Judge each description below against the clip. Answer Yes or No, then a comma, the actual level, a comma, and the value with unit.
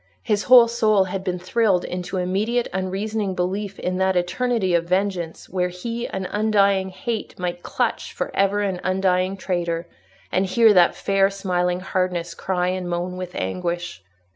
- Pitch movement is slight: Yes, narrow, 2.0 semitones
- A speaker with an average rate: Yes, average, 160 wpm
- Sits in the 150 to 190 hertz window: Yes, medium, 185 Hz